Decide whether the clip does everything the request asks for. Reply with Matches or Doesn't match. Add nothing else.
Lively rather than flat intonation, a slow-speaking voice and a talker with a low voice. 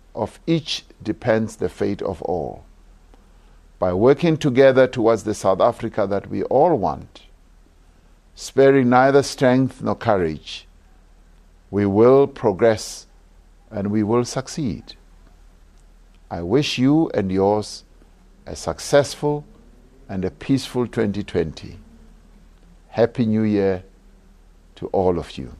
Matches